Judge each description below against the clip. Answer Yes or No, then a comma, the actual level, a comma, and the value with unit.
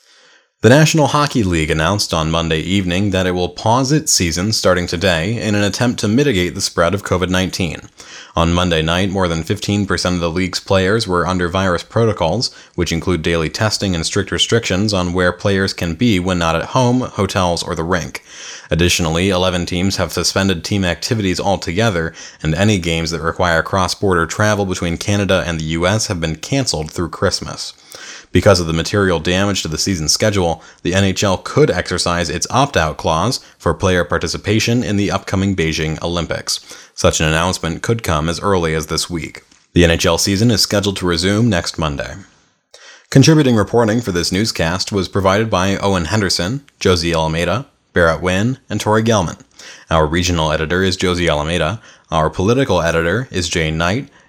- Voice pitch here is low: Yes, very low, 90 Hz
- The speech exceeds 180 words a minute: No, average, 175 wpm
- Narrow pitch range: No, average, 3.3 semitones